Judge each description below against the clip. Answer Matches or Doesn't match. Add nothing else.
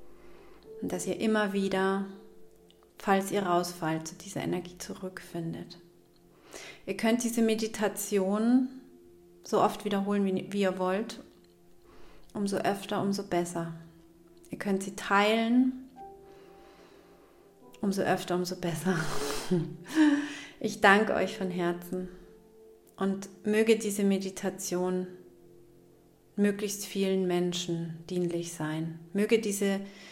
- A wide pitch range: Doesn't match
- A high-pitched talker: Matches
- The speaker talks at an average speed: Doesn't match